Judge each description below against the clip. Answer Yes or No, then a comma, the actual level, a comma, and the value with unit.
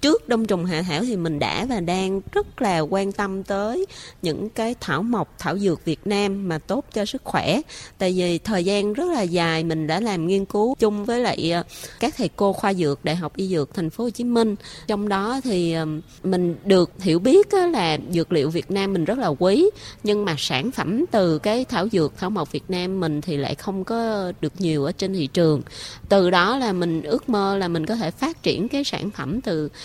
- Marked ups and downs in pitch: No, average, 4.9 semitones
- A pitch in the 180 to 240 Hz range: Yes, high, 190 Hz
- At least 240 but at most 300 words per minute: No, average, 225 wpm